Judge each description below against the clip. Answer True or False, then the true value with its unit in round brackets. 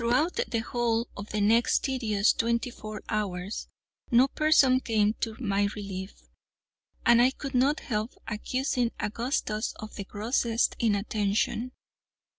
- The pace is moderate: False (130 wpm)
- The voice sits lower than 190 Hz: False (225 Hz)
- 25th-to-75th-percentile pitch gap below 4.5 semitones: True (2.9 semitones)